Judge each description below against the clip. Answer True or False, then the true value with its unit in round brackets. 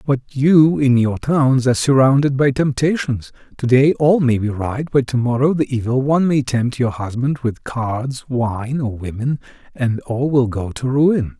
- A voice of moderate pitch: False (130 Hz)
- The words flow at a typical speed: True (180 wpm)